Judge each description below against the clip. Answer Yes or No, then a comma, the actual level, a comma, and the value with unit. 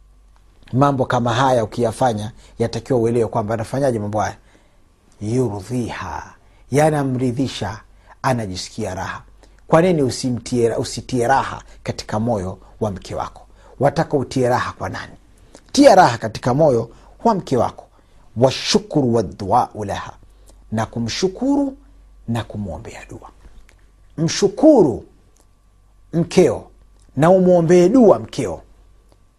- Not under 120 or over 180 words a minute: No, slow, 100 wpm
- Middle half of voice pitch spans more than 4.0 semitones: Yes, wide, 5.5 semitones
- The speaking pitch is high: No, low, 115 Hz